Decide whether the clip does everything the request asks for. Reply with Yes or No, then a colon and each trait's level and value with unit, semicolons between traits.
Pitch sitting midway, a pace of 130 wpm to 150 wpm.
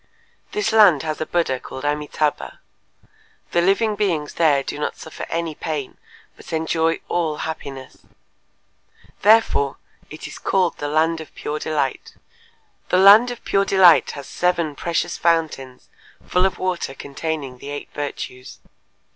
Yes: medium, 160 Hz; average, 140 wpm